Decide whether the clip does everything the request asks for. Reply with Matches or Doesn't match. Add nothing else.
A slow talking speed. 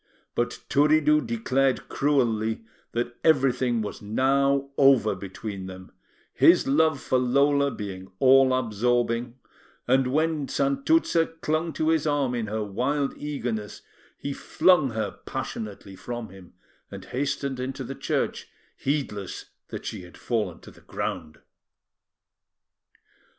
Matches